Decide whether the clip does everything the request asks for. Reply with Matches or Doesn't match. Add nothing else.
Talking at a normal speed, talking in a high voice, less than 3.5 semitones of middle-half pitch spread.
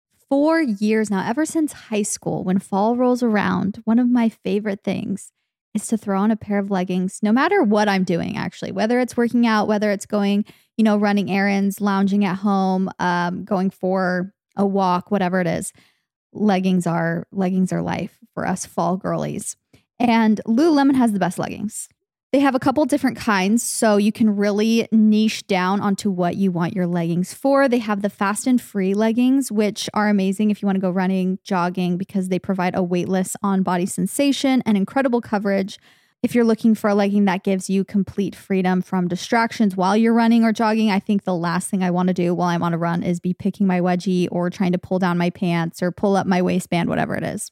Doesn't match